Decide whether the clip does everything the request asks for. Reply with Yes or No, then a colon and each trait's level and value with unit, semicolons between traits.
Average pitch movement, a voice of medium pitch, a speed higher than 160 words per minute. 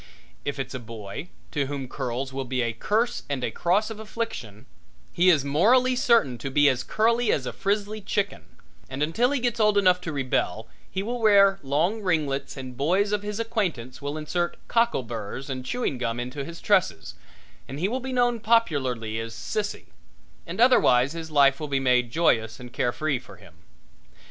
No: wide, 8.4 semitones; medium, 155 Hz; average, 190 wpm